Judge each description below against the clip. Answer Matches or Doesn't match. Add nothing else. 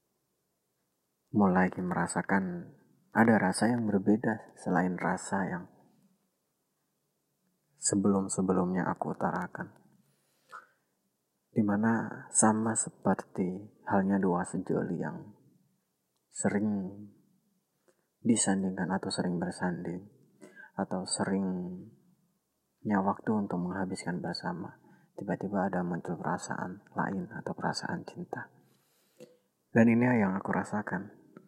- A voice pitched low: Matches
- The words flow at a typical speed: Doesn't match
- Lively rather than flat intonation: Doesn't match